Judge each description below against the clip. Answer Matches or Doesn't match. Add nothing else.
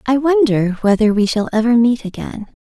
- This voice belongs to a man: Doesn't match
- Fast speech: Doesn't match